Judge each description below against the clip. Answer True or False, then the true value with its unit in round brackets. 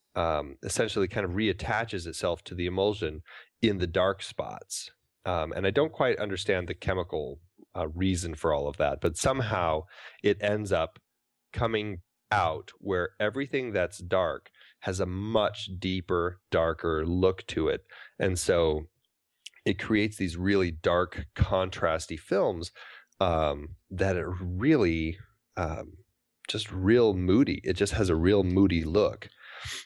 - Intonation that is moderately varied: True (3.2 semitones)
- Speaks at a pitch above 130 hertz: False (95 Hz)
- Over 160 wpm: False (140 wpm)